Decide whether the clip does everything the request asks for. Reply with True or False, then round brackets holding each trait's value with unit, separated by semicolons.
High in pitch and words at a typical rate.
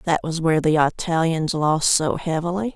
False (165 Hz; 175 wpm)